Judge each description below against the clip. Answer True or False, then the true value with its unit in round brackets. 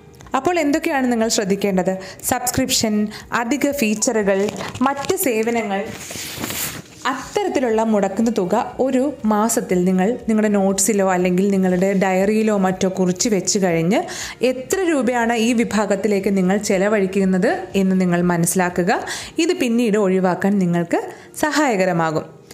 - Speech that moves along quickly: False (100 wpm)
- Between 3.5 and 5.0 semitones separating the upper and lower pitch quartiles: True (4.5 semitones)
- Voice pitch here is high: True (210 Hz)